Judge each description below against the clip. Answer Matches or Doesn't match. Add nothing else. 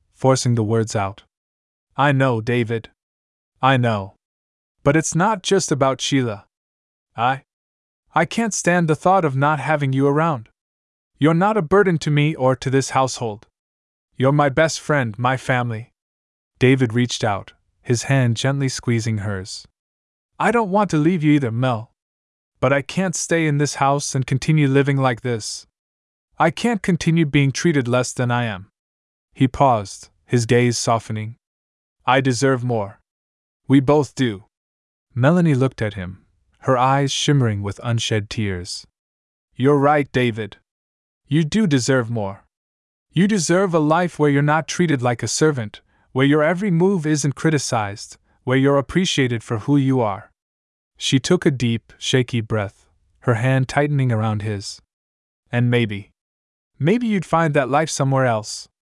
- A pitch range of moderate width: Doesn't match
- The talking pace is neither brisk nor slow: Matches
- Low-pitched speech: Matches